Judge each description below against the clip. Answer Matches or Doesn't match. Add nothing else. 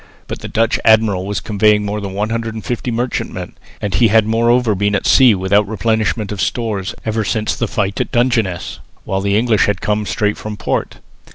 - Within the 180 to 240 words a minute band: Matches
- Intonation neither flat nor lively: Doesn't match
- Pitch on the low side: Matches